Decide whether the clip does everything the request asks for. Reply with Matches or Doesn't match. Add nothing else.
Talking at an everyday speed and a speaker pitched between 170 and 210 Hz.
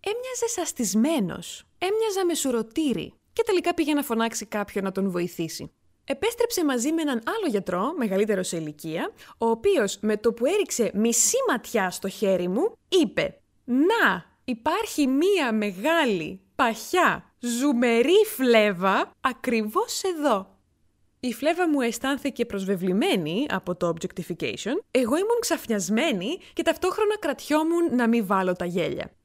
Doesn't match